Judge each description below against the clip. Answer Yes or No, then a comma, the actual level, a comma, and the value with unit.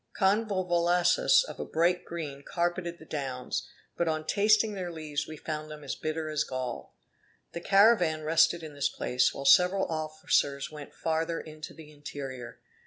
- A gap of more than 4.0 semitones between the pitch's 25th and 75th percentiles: No, average, 3.0 semitones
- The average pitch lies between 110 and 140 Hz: No, medium, 160 Hz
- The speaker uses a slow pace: No, average, 160 wpm